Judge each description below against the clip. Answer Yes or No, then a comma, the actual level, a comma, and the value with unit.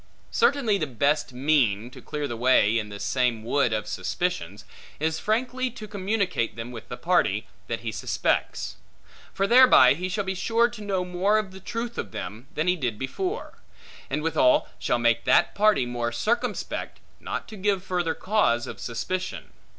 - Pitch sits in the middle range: Yes, medium, 155 Hz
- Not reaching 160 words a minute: No, average, 175 wpm